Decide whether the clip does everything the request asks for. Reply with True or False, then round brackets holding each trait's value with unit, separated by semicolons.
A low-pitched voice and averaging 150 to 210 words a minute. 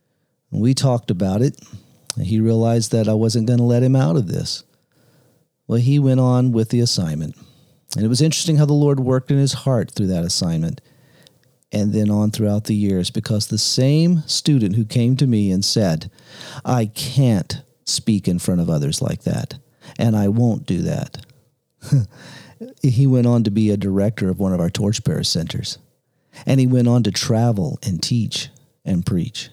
True (125 Hz; 185 wpm)